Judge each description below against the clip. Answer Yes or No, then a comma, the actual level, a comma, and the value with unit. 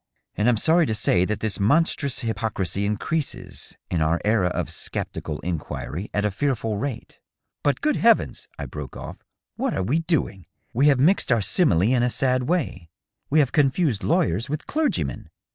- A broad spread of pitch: Yes, wide, 6.9 semitones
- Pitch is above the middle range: No, low, 120 Hz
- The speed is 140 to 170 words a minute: No, average, 180 wpm